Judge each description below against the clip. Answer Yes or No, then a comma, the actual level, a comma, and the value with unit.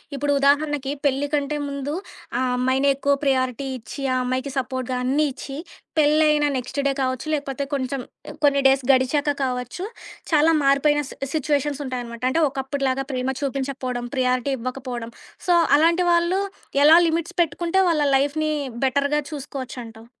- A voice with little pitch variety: Yes, narrow, 2.3 semitones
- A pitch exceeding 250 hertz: Yes, very high, 275 Hz